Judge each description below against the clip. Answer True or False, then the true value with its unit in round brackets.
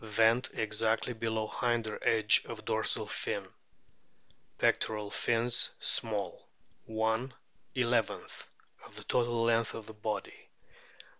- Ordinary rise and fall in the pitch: False (1.2 semitones)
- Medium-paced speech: False (90 wpm)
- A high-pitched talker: False (115 Hz)